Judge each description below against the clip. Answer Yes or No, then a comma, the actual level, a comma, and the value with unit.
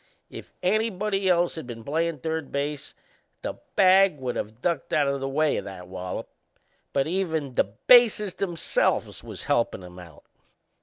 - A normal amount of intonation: No, wide, 6.7 semitones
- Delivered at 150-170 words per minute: Yes, average, 160 wpm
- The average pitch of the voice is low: No, medium, 155 Hz